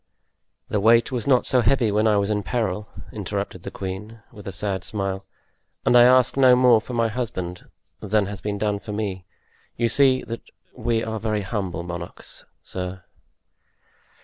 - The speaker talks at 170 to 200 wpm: Yes, average, 175 wpm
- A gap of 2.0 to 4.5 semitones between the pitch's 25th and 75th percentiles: Yes, average, 3.3 semitones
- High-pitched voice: No, low, 105 Hz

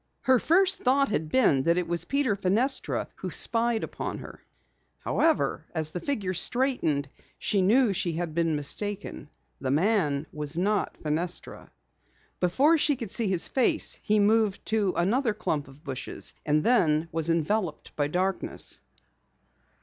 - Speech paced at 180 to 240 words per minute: No, average, 150 wpm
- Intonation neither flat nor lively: No, wide, 6.6 semitones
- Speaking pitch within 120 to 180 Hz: No, high, 190 Hz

